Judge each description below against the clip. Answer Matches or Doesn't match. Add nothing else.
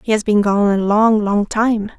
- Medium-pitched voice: Doesn't match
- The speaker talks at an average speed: Doesn't match